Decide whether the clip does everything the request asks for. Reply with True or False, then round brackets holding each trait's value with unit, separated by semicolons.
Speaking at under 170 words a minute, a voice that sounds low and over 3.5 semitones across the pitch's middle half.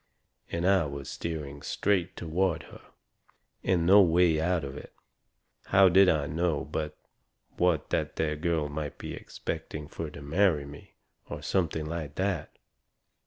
False (150 wpm; 80 Hz; 3.2 semitones)